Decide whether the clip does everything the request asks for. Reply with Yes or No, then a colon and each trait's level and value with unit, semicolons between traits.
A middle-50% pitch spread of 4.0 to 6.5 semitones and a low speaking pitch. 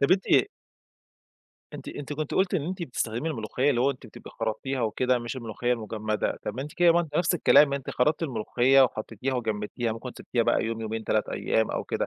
Yes: average, 4.6 semitones; low, 125 Hz